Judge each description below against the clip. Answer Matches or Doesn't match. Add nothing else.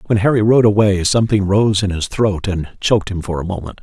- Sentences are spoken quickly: Matches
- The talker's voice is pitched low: Matches